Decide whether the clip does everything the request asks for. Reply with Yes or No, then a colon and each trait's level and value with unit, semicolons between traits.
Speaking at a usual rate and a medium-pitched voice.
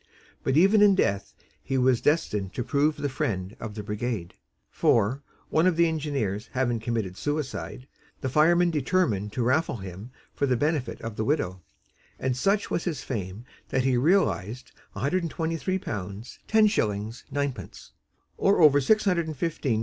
No: average, 165 wpm; low, 130 Hz